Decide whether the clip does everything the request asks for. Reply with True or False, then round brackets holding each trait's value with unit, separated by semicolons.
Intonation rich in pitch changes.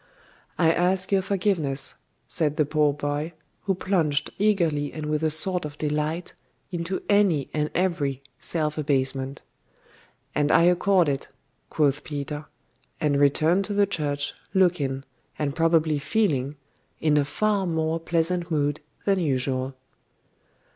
False (3.5 semitones)